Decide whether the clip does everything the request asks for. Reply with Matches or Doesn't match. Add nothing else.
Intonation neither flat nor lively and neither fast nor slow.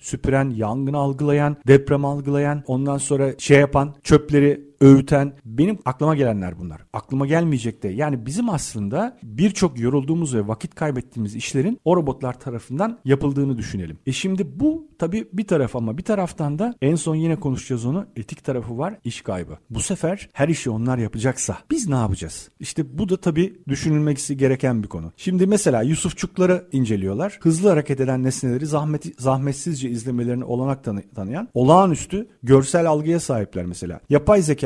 Doesn't match